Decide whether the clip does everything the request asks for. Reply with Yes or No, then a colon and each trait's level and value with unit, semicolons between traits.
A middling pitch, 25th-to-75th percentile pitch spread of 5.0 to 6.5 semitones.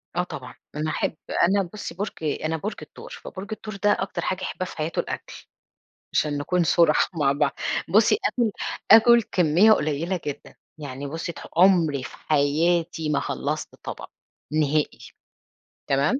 No: medium, 165 Hz; average, 4.2 semitones